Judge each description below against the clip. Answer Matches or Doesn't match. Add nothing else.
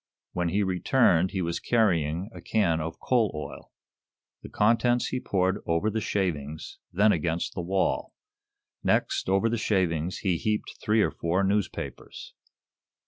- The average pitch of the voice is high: Doesn't match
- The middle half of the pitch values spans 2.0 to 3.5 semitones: Doesn't match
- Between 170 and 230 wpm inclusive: Doesn't match